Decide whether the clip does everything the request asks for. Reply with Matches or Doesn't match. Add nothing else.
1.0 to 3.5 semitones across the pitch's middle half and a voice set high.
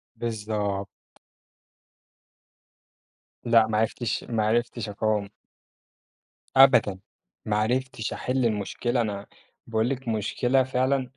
Doesn't match